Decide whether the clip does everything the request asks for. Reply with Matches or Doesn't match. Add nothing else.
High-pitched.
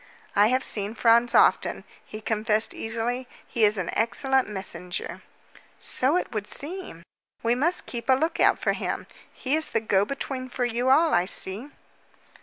Matches